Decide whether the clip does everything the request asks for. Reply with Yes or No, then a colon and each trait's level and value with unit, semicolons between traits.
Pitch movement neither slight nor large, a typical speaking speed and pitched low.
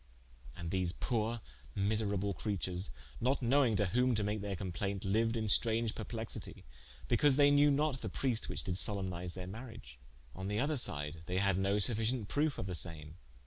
Yes: average, 4.1 semitones; average, 180 wpm; low, 105 Hz